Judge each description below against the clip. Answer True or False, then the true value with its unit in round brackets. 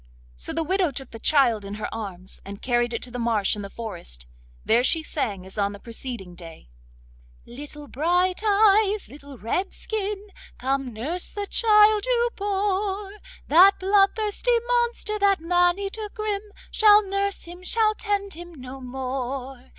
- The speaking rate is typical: True (160 wpm)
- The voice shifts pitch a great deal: True (9.0 semitones)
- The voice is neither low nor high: False (335 Hz)